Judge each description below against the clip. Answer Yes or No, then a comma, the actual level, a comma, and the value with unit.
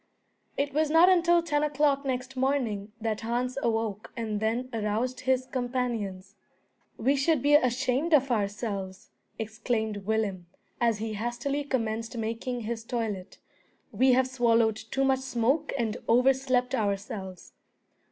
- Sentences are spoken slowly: Yes, slow, 130 wpm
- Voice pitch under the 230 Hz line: No, high, 240 Hz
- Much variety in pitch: No, average, 3.4 semitones